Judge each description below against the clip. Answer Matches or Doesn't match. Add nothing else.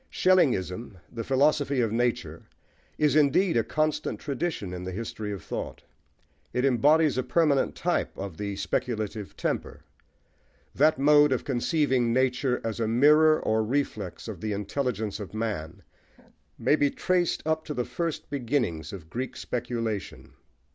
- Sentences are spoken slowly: Doesn't match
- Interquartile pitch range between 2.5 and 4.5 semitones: Doesn't match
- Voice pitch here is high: Doesn't match